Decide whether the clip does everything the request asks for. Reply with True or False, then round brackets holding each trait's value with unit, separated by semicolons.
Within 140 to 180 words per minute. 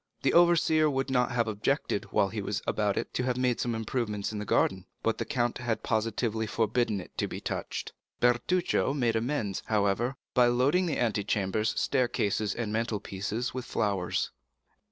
True (175 wpm)